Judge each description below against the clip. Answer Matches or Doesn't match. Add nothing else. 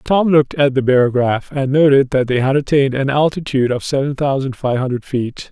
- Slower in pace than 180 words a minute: Doesn't match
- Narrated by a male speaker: Matches